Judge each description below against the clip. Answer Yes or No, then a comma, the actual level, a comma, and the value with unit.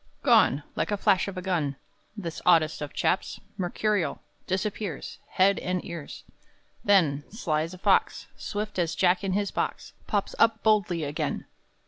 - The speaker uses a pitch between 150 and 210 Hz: Yes, medium, 185 Hz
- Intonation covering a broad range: No, average, 3.7 semitones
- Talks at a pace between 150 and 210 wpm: Yes, average, 160 wpm